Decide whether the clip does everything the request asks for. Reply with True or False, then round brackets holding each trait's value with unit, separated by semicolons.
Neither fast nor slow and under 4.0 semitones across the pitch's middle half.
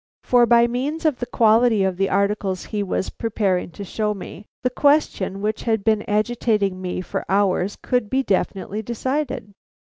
True (170 wpm; 3.6 semitones)